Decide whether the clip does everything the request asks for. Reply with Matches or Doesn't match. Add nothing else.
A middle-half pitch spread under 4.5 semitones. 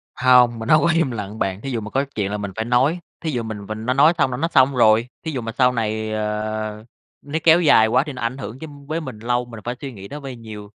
Matches